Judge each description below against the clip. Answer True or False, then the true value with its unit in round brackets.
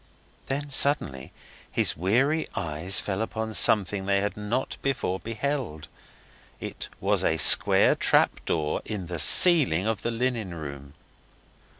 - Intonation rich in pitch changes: True (6.9 semitones)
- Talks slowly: True (130 wpm)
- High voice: False (105 Hz)